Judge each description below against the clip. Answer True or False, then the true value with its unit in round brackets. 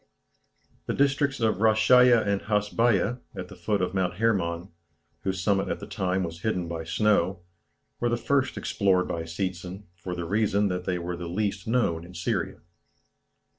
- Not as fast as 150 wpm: False (170 wpm)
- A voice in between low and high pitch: False (95 Hz)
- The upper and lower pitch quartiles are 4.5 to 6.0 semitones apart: False (3.7 semitones)